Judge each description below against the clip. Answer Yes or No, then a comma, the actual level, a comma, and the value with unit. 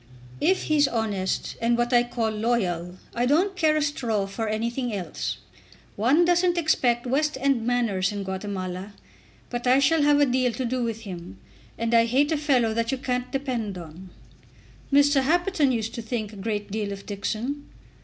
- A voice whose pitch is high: Yes, high, 240 Hz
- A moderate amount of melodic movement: Yes, average, 4.8 semitones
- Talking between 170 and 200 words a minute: Yes, average, 180 wpm